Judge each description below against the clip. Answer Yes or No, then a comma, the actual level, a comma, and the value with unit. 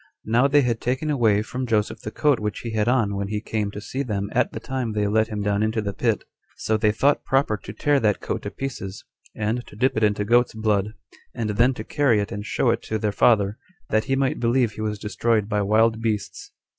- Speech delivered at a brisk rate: Yes, fast, 235 wpm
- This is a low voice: Yes, low, 110 Hz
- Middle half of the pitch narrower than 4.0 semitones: Yes, average, 2.8 semitones